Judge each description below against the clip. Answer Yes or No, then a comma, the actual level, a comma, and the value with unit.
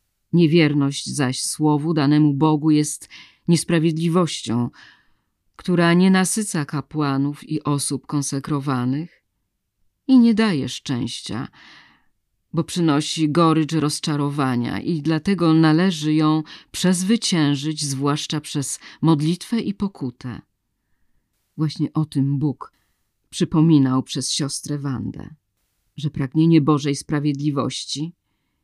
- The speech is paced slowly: Yes, slow, 90 wpm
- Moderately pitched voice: Yes, medium, 150 Hz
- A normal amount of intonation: Yes, average, 3.0 semitones